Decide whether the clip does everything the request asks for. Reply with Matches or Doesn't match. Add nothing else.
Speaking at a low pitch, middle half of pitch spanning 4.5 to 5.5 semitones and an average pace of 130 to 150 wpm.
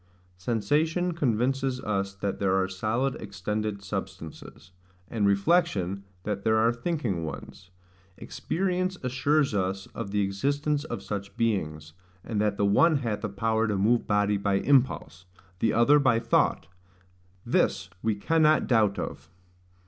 Matches